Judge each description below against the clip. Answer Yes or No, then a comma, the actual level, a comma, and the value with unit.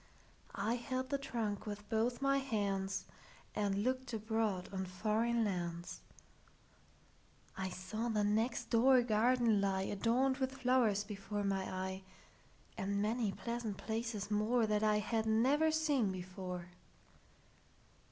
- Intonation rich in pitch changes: No, average, 3.5 semitones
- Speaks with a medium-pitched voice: No, high, 215 Hz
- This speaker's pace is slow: Yes, slow, 110 wpm